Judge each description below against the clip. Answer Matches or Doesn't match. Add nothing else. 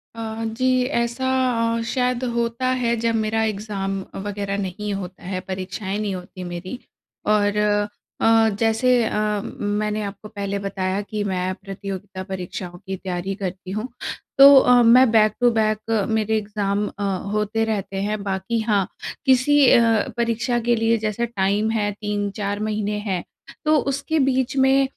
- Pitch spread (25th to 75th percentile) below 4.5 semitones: Matches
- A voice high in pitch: Matches